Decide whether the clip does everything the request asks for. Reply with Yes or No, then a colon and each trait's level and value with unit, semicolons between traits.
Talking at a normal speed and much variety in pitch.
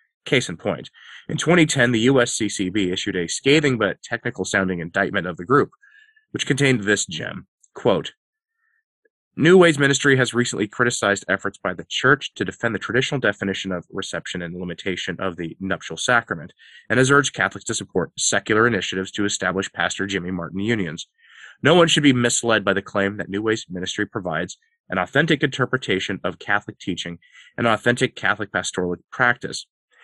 Yes: average, 165 wpm; wide, 6.6 semitones